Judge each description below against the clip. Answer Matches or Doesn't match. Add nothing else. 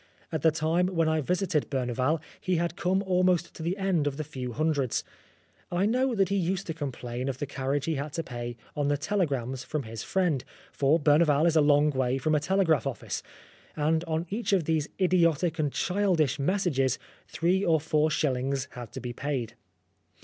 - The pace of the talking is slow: Doesn't match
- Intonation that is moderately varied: Matches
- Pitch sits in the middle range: Matches